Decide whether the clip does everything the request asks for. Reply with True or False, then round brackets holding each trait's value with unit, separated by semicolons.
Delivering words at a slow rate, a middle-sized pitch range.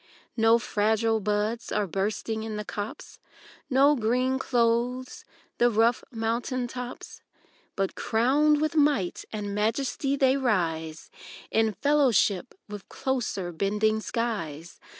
True (115 wpm; 3.5 semitones)